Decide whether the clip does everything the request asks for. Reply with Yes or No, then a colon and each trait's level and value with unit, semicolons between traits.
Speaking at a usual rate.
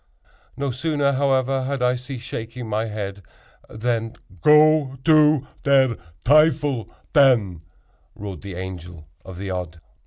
No: slow, 125 wpm